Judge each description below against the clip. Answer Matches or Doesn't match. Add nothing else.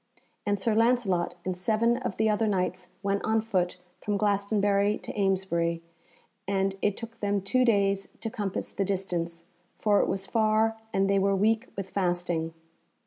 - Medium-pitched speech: Doesn't match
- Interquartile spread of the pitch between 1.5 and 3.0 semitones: Matches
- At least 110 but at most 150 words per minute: Doesn't match